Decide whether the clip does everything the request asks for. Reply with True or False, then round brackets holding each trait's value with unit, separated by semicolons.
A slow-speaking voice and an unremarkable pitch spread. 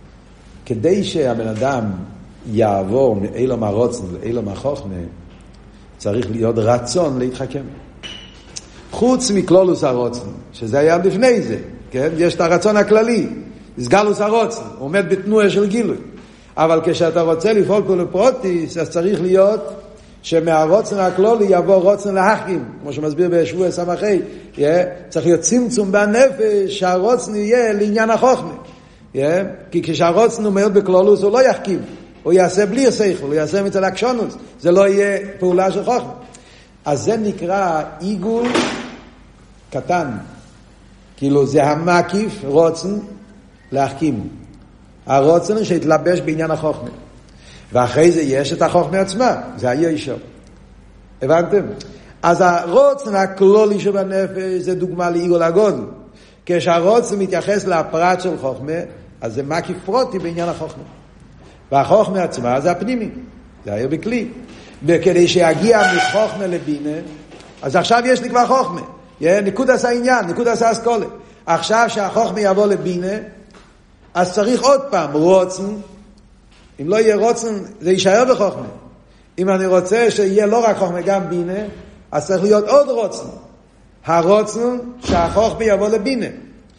False (125 wpm; 4.4 semitones)